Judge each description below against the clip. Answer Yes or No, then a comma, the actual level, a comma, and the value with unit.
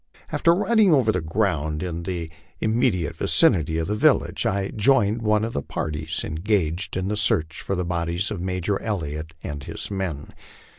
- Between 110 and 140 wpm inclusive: No, average, 170 wpm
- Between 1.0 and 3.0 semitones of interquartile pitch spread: No, average, 4.8 semitones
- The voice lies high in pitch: No, very low, 90 Hz